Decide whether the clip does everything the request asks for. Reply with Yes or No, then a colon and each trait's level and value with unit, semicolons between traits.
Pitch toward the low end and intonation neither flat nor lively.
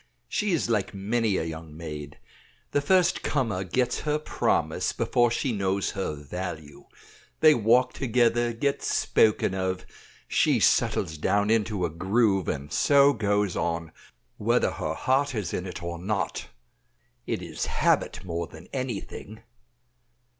No: low, 100 Hz; wide, 5.9 semitones